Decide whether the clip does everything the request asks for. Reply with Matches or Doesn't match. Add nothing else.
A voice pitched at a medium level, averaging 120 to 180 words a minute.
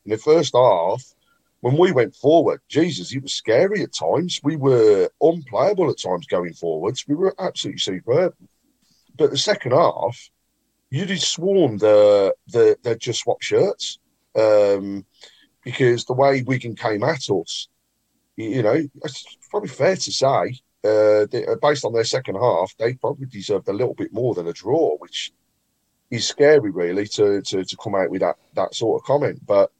Matches